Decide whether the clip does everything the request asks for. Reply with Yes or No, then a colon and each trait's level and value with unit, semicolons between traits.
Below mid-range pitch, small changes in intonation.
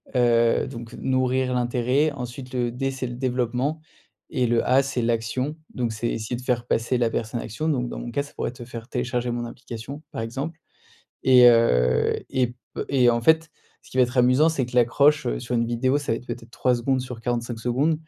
Yes: low, 125 Hz; narrow, 1.9 semitones